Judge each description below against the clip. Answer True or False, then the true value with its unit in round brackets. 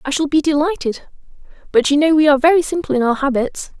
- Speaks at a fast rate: True (220 wpm)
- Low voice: False (290 Hz)